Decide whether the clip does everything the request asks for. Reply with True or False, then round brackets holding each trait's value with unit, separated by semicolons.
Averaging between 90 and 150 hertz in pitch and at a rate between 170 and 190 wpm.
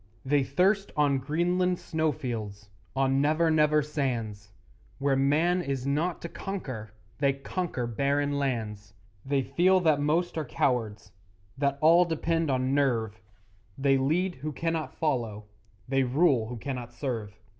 False (140 Hz; 135 wpm)